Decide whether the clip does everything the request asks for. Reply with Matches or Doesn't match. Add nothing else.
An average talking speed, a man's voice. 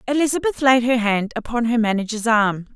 Doesn't match